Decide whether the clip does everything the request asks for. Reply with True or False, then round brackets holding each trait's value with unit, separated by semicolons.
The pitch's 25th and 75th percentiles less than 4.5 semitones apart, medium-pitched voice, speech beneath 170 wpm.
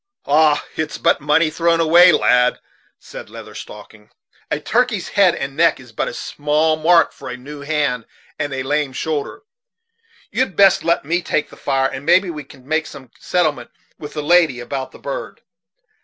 False (3.7 semitones; 150 Hz; 180 wpm)